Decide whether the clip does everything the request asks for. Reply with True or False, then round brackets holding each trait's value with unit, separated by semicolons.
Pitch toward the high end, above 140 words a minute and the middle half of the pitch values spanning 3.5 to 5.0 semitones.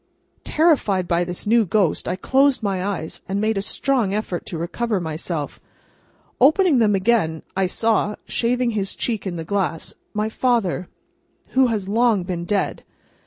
True (205 Hz; 160 wpm; 4.5 semitones)